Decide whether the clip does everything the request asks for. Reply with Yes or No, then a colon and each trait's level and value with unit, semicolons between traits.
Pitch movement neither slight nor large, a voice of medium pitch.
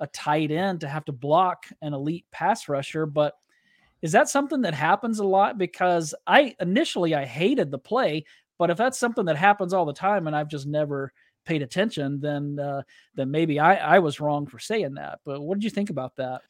Yes: average, 5.0 semitones; medium, 155 Hz